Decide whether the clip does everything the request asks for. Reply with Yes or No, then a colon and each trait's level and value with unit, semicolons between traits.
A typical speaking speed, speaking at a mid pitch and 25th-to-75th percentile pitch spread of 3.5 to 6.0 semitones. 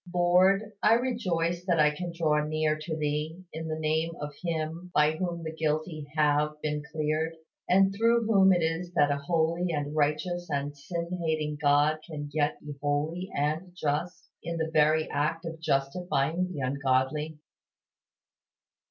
No: average, 160 wpm; medium, 160 Hz; average, 2.7 semitones